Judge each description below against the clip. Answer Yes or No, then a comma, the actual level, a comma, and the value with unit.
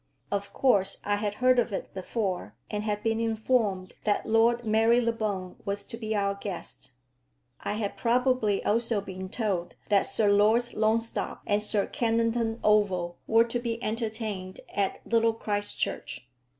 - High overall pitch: Yes, high, 215 Hz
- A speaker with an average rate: Yes, average, 150 wpm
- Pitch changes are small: Yes, narrow, 2.3 semitones